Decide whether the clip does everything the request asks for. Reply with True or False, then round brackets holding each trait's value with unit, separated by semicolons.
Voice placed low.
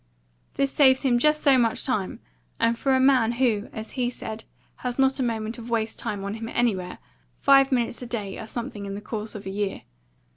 False (235 Hz)